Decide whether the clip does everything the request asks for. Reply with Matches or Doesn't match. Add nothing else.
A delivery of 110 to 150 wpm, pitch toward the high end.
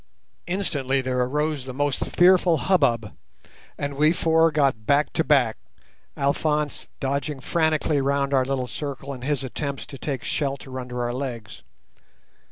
Doesn't match